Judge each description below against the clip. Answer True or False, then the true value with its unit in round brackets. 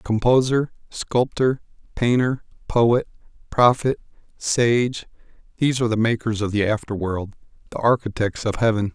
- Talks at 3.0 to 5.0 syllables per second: True (4.7 syllables/s)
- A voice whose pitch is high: False (115 Hz)